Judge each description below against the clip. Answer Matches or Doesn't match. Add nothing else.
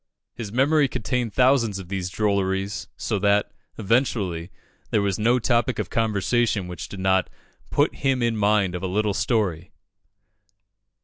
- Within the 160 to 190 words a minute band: Doesn't match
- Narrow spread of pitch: Doesn't match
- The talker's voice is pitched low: Matches